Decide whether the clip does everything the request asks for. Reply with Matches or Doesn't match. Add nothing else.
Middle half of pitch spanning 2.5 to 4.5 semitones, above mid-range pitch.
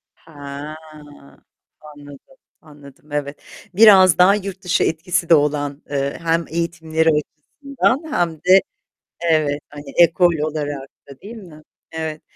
Doesn't match